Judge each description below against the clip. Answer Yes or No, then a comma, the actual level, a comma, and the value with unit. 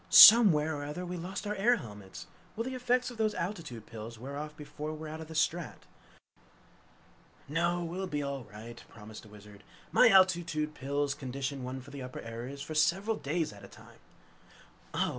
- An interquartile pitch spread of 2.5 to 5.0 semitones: No, wide, 5.6 semitones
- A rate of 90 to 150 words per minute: No, average, 185 wpm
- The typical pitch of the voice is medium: Yes, medium, 150 Hz